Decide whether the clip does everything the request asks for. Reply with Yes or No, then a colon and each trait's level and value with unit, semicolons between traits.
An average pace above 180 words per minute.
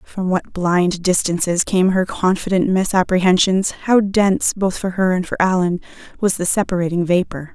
No: average, 160 wpm